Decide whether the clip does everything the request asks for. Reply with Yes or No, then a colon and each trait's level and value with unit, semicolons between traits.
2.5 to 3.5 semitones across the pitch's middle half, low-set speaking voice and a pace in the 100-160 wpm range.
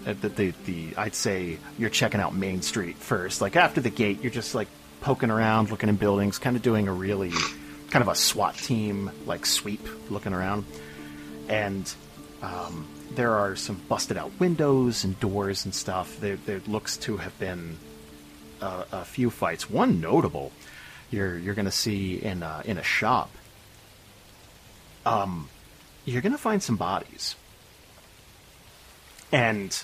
No: average, 4.0 semitones; low, 100 Hz; average, 155 wpm